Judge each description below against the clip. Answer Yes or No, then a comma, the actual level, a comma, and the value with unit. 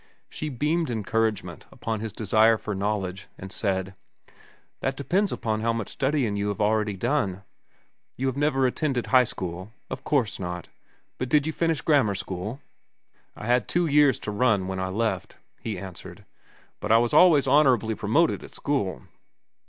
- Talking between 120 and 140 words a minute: No, average, 165 wpm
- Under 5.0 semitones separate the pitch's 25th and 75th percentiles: No, wide, 5.4 semitones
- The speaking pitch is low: Yes, low, 115 Hz